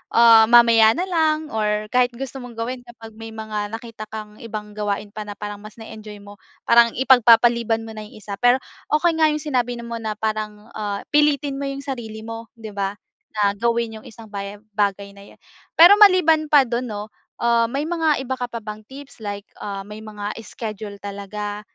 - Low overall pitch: No, high, 225 Hz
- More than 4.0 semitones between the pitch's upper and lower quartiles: No, average, 3.0 semitones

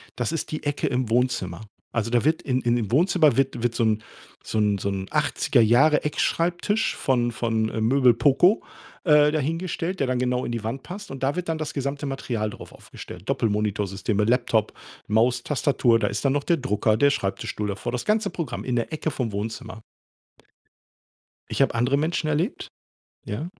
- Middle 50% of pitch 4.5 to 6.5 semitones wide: Yes, average, 5.0 semitones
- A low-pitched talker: Yes, low, 125 Hz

